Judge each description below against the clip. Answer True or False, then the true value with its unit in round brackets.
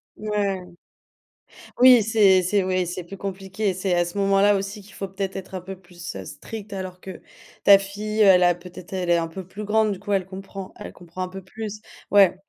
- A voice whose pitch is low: False (195 Hz)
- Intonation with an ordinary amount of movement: False (1.9 semitones)